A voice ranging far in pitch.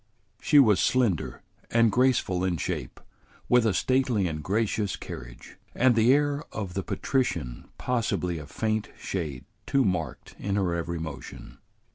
Yes: wide, 6.2 semitones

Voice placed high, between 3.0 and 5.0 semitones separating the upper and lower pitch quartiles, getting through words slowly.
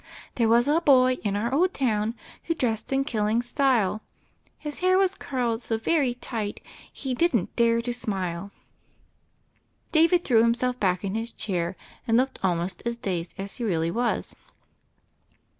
No: high, 235 Hz; average, 4.2 semitones; average, 165 wpm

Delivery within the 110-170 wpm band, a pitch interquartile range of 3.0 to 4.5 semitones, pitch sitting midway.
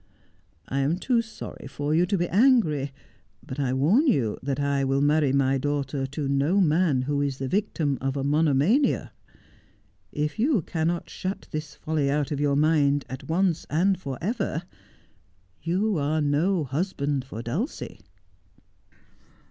Yes: average, 155 wpm; average, 4.2 semitones; medium, 150 Hz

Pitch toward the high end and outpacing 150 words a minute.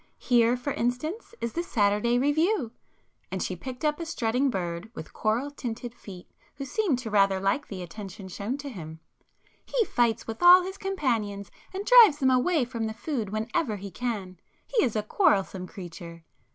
Yes: high, 235 Hz; average, 170 wpm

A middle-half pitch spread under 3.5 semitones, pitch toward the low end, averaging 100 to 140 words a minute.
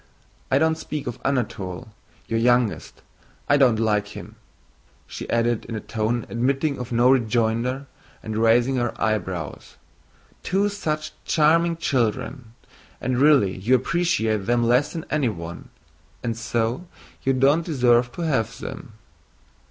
No: average, 3.9 semitones; low, 120 Hz; slow, 135 wpm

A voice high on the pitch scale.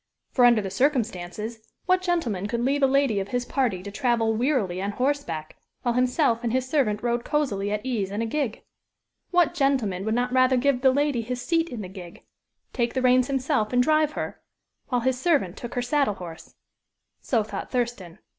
Yes: high, 245 Hz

